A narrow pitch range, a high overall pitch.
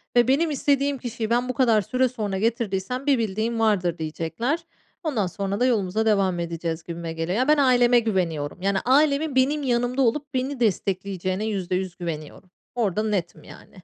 No: wide, 5.4 semitones; high, 220 Hz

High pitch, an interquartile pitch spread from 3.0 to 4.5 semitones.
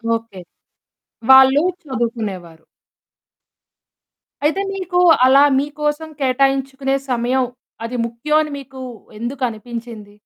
Yes: very high, 265 Hz; average, 3.5 semitones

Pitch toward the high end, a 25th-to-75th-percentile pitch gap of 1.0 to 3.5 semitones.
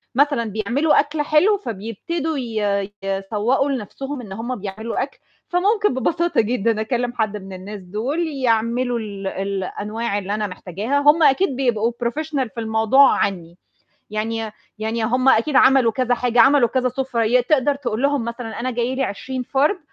No: high, 240 Hz; average, 4.2 semitones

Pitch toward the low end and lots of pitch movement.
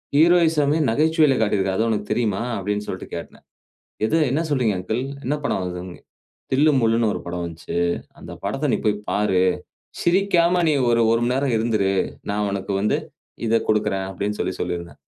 Yes: low, 110 Hz; wide, 6.3 semitones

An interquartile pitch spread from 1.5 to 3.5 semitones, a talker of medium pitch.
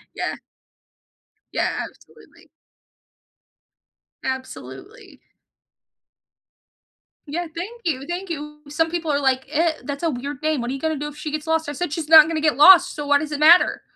No: narrow, 2.4 semitones; very high, 305 Hz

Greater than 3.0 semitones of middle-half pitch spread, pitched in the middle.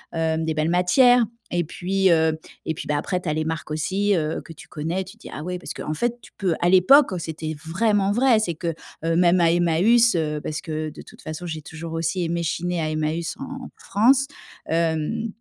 Yes: average, 3.6 semitones; medium, 170 Hz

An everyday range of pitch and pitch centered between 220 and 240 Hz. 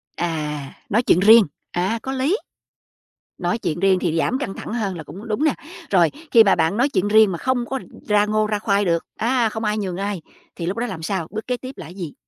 No: average, 4.5 semitones; high, 205 Hz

